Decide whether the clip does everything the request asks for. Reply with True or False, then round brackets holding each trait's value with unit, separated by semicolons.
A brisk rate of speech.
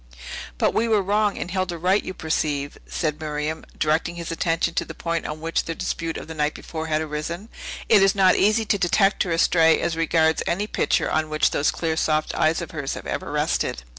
True (220 wpm)